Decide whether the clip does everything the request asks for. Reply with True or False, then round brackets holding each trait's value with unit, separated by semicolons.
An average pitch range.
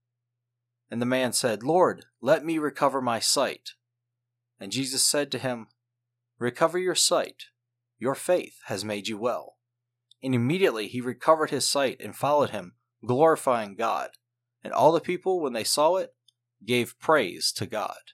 False (2.0 semitones)